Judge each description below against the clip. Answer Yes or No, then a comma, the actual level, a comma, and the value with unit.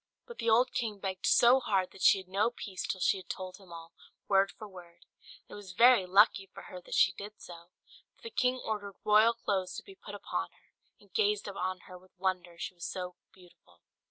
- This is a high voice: Yes, high, 195 Hz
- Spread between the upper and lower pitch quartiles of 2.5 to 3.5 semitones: Yes, average, 3.1 semitones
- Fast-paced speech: Yes, fast, 225 wpm